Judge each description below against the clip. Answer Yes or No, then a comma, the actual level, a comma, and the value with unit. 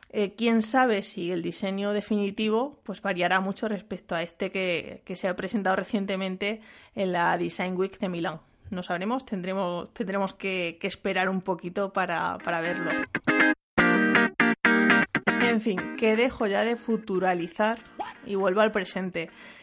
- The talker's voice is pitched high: Yes, high, 195 Hz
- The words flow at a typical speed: Yes, average, 145 wpm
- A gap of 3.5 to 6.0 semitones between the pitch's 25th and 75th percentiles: No, average, 2.8 semitones